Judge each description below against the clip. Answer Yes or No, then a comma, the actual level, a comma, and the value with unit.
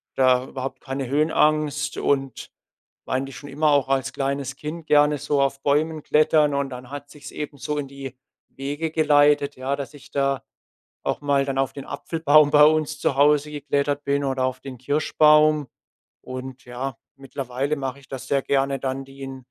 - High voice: No, medium, 140 Hz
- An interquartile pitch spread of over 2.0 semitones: No, narrow, 1.6 semitones